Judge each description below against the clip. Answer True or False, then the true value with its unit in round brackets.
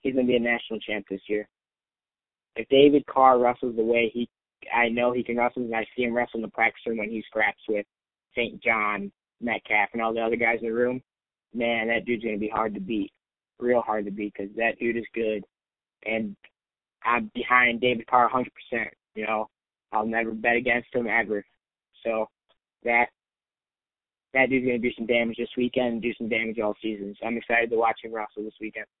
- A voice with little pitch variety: True (1.9 semitones)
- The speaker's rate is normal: False (215 wpm)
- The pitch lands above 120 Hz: False (115 Hz)